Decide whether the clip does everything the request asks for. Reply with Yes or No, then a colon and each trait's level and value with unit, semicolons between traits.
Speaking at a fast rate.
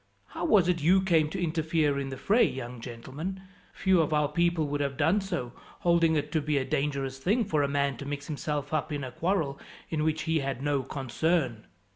Yes: fast, 215 wpm